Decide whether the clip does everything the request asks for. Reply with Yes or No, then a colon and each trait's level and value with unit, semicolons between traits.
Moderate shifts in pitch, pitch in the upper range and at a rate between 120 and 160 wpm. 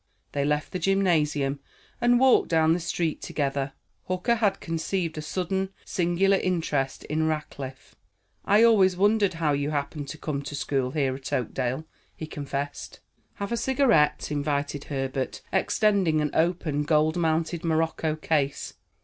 No: average, 4.3 semitones; medium, 160 Hz; average, 145 wpm